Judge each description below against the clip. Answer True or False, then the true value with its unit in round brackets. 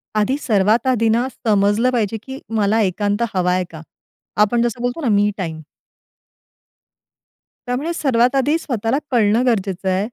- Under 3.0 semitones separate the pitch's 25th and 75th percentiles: False (3.5 semitones)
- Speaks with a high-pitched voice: True (225 Hz)